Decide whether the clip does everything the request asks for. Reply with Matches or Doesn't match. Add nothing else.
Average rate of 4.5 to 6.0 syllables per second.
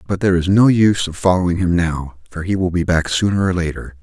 Doesn't match